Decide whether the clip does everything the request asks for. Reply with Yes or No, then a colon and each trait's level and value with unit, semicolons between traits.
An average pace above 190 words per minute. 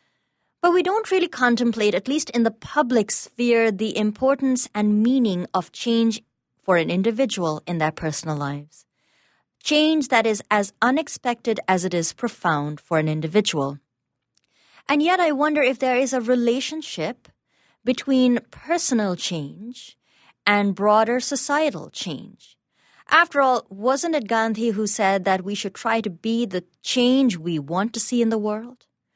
No: average, 150 wpm